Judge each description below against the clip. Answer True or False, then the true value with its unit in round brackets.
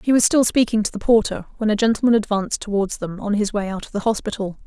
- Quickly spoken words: True (255 wpm)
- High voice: True (215 Hz)